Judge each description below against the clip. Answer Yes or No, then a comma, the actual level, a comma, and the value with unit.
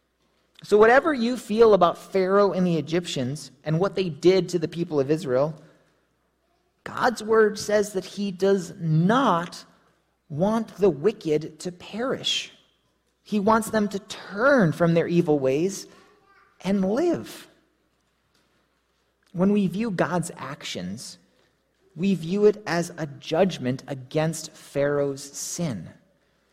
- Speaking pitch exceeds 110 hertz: Yes, medium, 185 Hz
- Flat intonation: No, average, 4.4 semitones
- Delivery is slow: Yes, slow, 125 wpm